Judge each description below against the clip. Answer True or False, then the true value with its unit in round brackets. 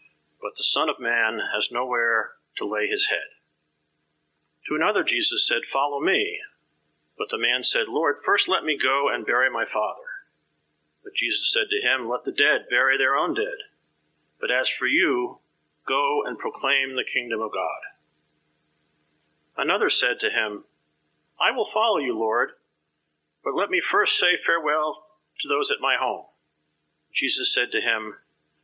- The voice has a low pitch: False (155 Hz)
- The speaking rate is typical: True (160 wpm)